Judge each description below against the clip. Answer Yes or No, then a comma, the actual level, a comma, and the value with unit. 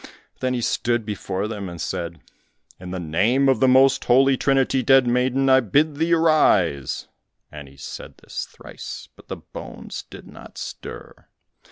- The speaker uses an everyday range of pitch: No, wide, 6.4 semitones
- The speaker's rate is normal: Yes, average, 165 wpm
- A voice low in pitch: Yes, low, 125 Hz